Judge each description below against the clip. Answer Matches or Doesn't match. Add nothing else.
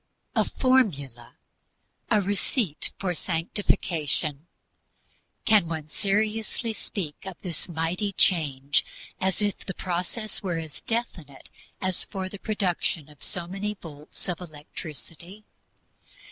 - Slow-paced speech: Matches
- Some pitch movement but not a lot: Matches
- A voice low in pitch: Doesn't match